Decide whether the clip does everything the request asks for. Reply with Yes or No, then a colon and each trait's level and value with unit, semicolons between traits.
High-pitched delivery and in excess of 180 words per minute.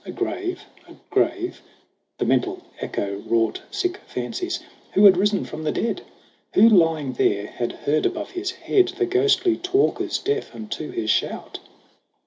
No: very high, 330 Hz; average, 150 wpm